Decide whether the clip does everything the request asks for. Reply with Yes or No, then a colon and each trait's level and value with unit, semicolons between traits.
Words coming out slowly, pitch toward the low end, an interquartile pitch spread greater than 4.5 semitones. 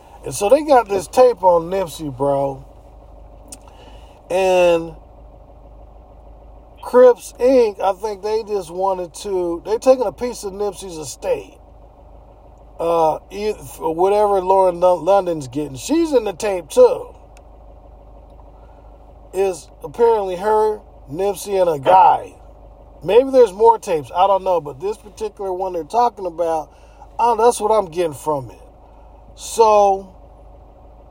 No: slow, 125 wpm; high, 195 Hz; average, 4.9 semitones